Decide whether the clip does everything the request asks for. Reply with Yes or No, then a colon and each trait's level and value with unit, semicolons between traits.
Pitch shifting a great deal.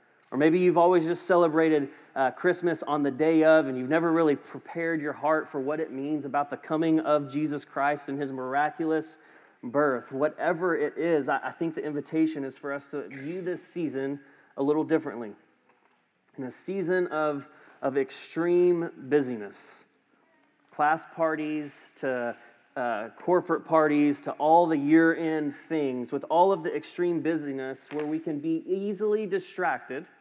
No: narrow, 2.6 semitones